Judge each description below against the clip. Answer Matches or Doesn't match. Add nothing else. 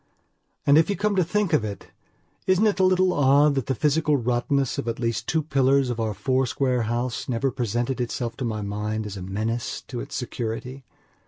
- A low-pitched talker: Matches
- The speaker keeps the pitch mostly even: Doesn't match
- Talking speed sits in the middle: Doesn't match